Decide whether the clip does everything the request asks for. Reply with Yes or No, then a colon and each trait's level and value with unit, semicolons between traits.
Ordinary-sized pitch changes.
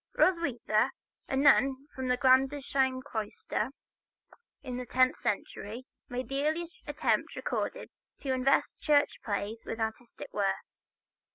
No: narrow, 2.3 semitones